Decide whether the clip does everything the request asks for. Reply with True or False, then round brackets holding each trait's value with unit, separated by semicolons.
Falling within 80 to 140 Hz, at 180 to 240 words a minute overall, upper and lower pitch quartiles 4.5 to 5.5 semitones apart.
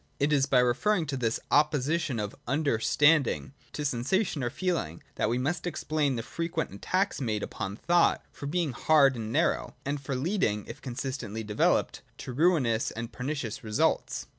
False (135 Hz; 165 wpm; 5.1 semitones)